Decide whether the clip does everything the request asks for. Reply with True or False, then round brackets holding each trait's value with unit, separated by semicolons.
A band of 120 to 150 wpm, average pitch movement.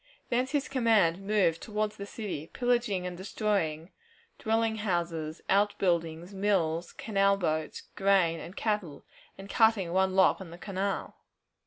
True (140 wpm; 3.8 semitones)